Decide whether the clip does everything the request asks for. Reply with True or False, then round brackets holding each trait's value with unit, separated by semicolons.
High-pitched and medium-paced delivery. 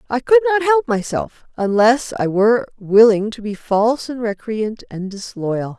True (230 Hz; 165 wpm)